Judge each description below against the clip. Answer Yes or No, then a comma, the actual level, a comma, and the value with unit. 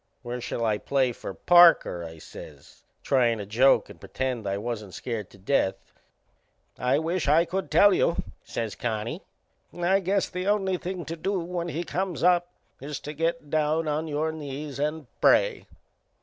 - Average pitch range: No, wide, 6.3 semitones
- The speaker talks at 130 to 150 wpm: No, average, 170 wpm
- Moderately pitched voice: Yes, medium, 150 Hz